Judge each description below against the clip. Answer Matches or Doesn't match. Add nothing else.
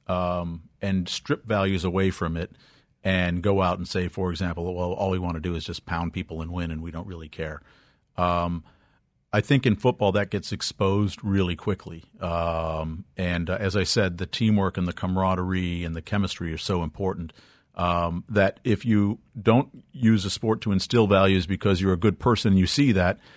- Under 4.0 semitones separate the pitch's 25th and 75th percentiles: Matches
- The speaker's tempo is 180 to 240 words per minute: Matches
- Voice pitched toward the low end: Matches